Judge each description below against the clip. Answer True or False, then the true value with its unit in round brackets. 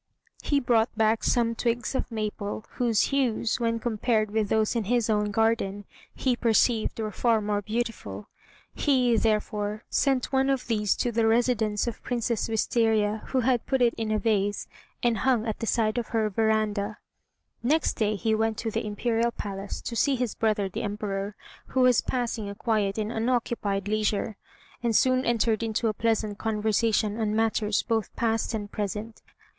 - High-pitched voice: True (225 Hz)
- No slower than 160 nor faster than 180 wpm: True (170 wpm)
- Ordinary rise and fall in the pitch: False (2.0 semitones)